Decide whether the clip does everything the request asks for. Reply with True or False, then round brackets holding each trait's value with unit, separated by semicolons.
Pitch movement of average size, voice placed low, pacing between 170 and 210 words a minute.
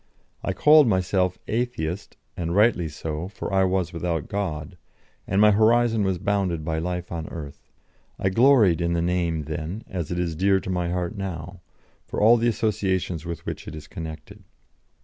True (3.5 semitones; 90 Hz; 175 wpm)